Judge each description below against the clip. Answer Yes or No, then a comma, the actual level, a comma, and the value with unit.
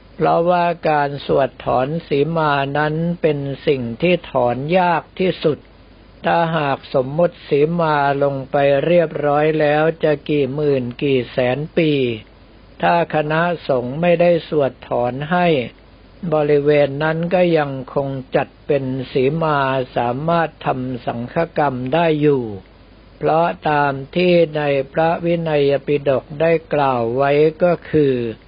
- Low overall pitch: No, medium, 145 Hz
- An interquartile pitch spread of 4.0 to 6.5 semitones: No, average, 3.4 semitones